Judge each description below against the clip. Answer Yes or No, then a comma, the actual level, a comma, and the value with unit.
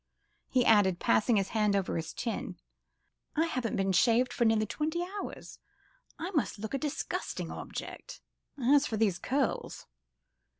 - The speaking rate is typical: Yes, average, 145 wpm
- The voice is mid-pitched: No, high, 230 Hz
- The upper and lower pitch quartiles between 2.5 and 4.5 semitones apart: No, average, 5.0 semitones